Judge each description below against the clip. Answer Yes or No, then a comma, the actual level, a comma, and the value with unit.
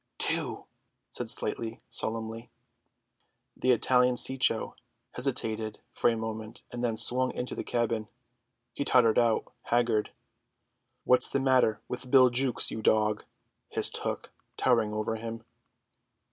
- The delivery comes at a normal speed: No, slow, 125 wpm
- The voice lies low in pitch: Yes, low, 115 Hz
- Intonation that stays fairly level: Yes, narrow, 2.2 semitones